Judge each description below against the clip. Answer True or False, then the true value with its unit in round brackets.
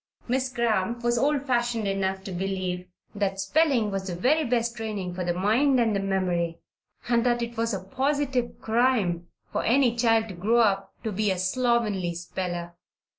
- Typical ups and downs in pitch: True (4.1 semitones)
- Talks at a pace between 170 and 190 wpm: True (175 wpm)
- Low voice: False (220 Hz)